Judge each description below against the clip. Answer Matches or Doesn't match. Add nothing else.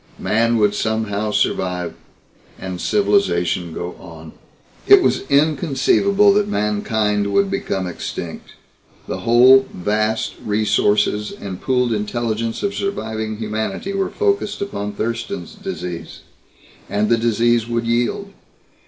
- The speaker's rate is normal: Doesn't match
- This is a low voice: Matches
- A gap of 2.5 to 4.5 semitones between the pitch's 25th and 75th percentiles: Doesn't match